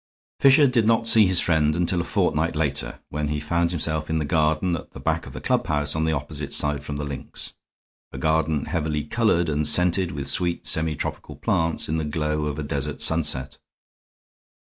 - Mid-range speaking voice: No, very low, 80 Hz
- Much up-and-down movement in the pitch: No, narrow, 2.4 semitones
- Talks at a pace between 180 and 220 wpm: Yes, average, 190 wpm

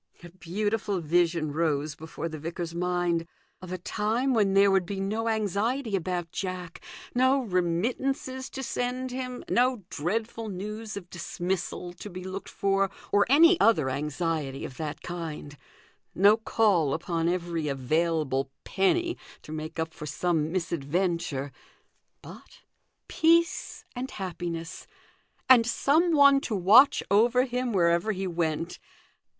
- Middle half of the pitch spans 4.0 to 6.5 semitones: Yes, wide, 5.4 semitones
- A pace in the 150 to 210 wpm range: No, slow, 135 wpm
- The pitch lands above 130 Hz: Yes, medium, 185 Hz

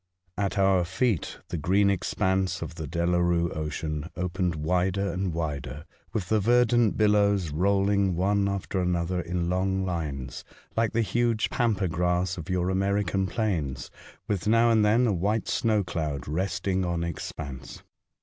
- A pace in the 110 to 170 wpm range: Yes, average, 150 wpm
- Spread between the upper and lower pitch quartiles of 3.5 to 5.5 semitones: No, average, 3.1 semitones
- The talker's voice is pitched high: No, very low, 95 Hz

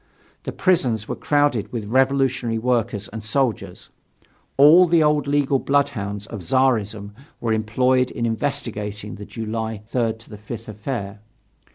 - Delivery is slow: Yes, slow, 130 wpm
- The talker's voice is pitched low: Yes, low, 115 Hz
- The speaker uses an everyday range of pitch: Yes, average, 3.9 semitones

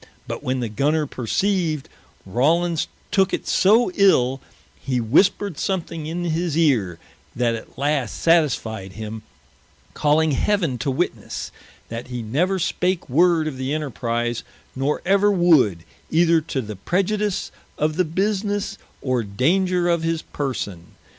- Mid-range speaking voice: Yes, medium, 155 Hz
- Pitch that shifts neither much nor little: No, wide, 6.2 semitones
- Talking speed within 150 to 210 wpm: No, slow, 135 wpm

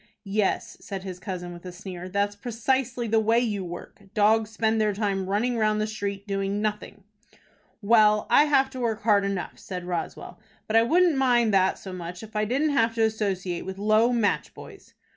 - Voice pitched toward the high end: Yes, high, 210 Hz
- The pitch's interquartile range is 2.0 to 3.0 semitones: Yes, narrow, 2.6 semitones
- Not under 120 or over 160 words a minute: No, average, 195 wpm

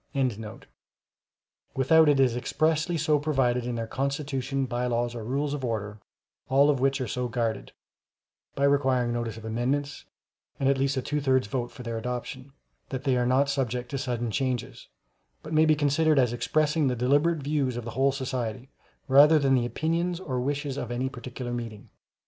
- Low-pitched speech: Yes, low, 130 Hz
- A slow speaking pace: No, average, 180 wpm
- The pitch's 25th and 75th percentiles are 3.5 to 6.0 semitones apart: No, average, 2.8 semitones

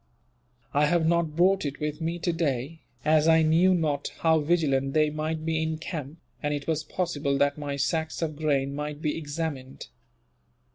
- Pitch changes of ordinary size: No, narrow, 2.0 semitones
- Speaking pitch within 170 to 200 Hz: No, medium, 155 Hz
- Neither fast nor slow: Yes, average, 175 wpm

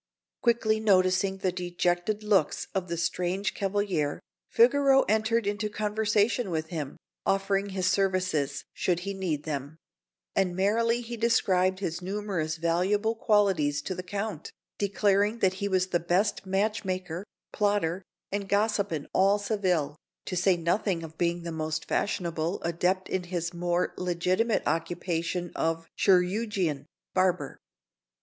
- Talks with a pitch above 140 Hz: Yes, medium, 185 Hz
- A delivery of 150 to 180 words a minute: No, slow, 135 wpm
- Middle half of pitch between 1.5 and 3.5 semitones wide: Yes, average, 3.2 semitones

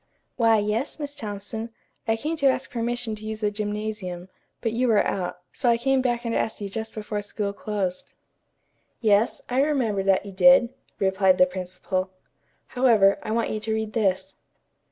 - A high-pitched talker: Yes, high, 215 Hz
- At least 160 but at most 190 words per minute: Yes, average, 175 wpm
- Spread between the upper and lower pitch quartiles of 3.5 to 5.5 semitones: No, average, 2.9 semitones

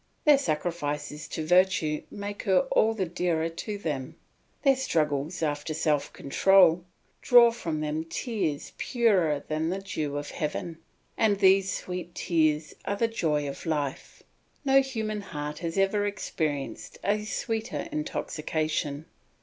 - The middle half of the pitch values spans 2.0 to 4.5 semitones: No, average, 5.1 semitones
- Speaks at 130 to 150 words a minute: Yes, slow, 135 wpm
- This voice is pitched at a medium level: Yes, medium, 170 Hz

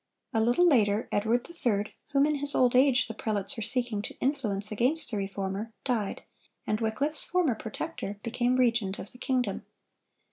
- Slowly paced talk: No, average, 170 wpm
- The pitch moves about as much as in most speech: Yes, average, 3.8 semitones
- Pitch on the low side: No, high, 235 Hz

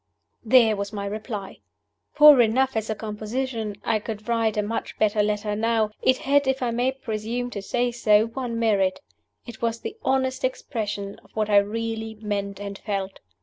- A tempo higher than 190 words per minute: No, average, 180 wpm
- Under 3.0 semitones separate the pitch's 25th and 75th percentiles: Yes, narrow, 2.6 semitones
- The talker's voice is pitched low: No, high, 220 Hz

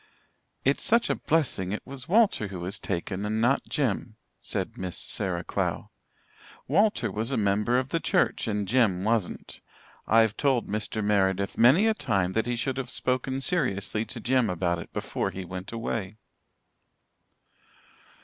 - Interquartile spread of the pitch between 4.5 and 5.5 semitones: Yes, average, 5.0 semitones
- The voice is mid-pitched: No, low, 110 Hz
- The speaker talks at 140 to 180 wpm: Yes, average, 160 wpm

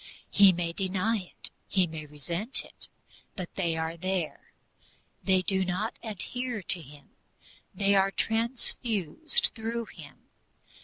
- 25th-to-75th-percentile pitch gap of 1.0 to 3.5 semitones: No, average, 4.6 semitones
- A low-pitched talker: No, high, 190 Hz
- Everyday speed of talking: No, slow, 125 wpm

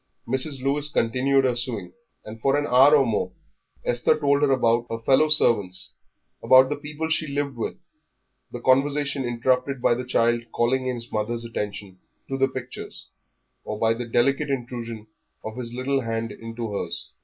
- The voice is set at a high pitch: No, low, 125 Hz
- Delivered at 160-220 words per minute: Yes, average, 165 wpm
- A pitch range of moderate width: Yes, average, 3.1 semitones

